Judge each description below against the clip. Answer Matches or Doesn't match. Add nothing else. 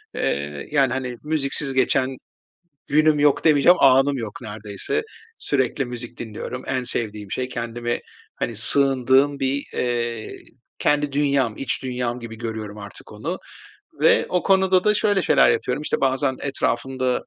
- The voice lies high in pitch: Doesn't match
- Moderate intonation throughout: Matches